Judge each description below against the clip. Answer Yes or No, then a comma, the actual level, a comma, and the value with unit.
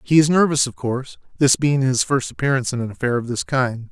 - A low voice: Yes, low, 130 Hz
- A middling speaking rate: No, fast, 245 wpm